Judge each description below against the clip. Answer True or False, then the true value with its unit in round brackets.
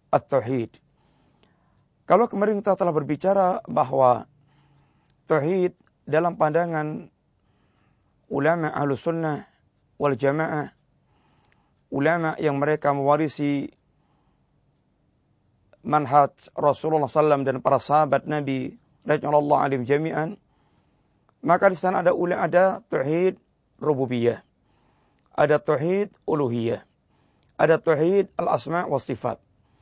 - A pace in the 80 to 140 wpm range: True (90 wpm)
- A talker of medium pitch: True (150 Hz)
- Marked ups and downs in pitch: False (3.1 semitones)